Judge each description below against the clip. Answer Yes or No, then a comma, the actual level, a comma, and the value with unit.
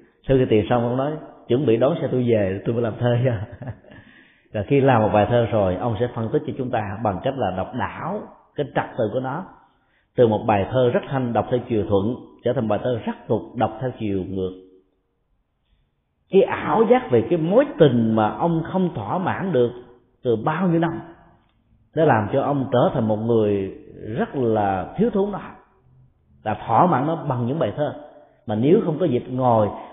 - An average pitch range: Yes, average, 4.7 semitones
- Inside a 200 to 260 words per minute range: Yes, average, 215 wpm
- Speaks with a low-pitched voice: Yes, low, 120 Hz